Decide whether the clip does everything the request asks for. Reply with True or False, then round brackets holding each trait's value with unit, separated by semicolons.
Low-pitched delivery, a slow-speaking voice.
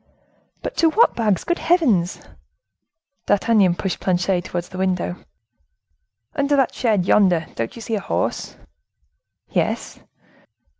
False (195 Hz; 120 wpm)